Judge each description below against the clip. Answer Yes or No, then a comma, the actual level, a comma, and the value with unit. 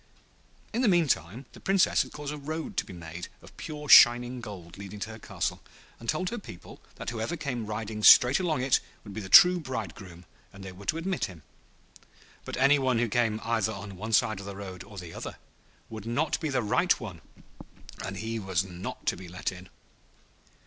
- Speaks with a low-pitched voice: Yes, low, 110 Hz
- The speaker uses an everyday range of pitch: No, wide, 6.2 semitones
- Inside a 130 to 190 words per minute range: No, fast, 205 wpm